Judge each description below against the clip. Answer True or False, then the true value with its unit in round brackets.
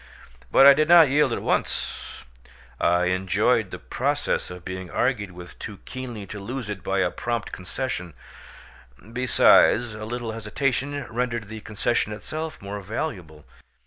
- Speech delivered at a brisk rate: False (145 wpm)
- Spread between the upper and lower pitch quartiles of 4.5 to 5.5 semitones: True (5.2 semitones)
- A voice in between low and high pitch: False (110 Hz)